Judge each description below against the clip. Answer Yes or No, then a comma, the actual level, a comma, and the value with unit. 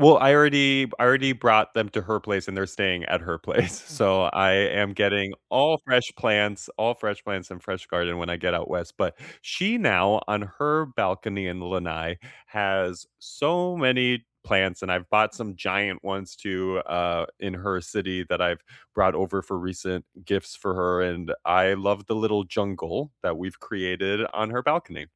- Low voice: Yes, low, 100 Hz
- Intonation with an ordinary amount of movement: Yes, average, 3.4 semitones